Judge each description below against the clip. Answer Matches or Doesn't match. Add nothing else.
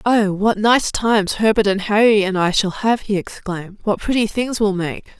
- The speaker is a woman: Matches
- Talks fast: Matches